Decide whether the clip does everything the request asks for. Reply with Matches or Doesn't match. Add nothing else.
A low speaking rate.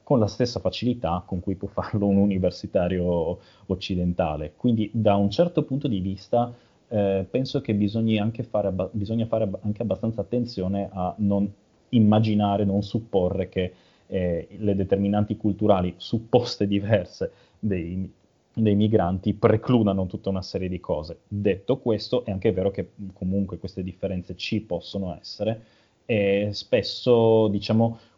Doesn't match